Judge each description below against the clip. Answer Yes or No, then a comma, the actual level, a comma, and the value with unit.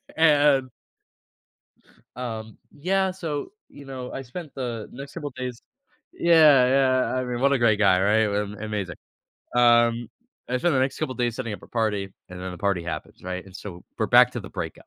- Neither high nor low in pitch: No, low, 125 Hz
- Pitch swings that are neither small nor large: Yes, average, 4.5 semitones